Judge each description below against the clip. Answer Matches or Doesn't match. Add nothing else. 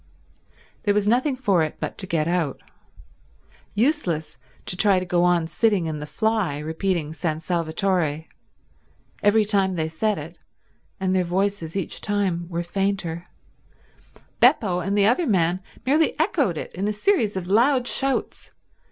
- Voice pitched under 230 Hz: Matches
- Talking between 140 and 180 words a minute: Matches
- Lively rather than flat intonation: Doesn't match